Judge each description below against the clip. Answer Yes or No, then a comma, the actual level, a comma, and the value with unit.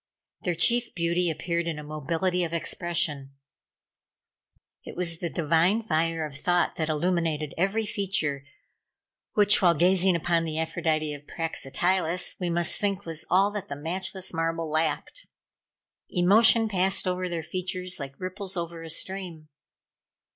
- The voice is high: No, medium, 170 Hz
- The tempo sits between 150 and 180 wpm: No, average, 140 wpm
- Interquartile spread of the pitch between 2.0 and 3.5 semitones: Yes, narrow, 2.5 semitones